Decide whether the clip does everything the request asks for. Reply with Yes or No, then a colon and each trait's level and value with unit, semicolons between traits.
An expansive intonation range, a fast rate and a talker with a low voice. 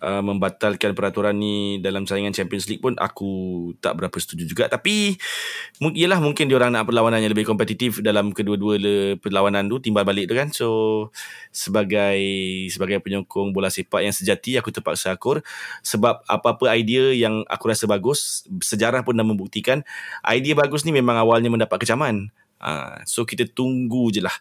No: average, 3.9 semitones; fast, 160 wpm; low, 110 Hz